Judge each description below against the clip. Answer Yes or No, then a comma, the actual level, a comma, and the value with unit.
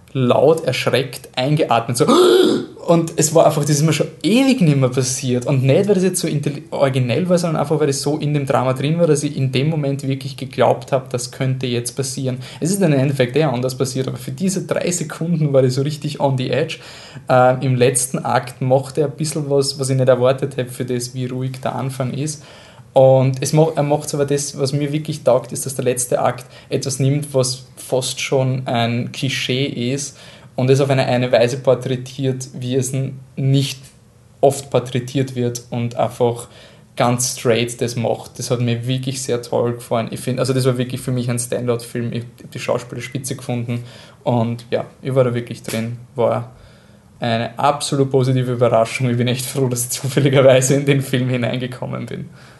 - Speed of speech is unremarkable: No, fast, 200 wpm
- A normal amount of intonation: No, narrow, 2.3 semitones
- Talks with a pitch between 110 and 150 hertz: Yes, low, 130 Hz